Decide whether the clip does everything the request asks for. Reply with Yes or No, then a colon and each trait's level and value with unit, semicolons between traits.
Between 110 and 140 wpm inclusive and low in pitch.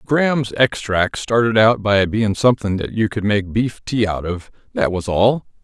No: average, 180 wpm; low, 105 Hz